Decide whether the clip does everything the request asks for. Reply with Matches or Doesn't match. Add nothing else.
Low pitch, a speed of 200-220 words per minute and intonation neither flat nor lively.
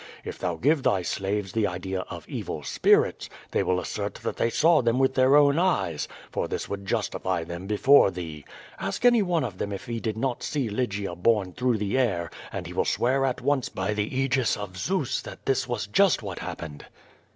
Doesn't match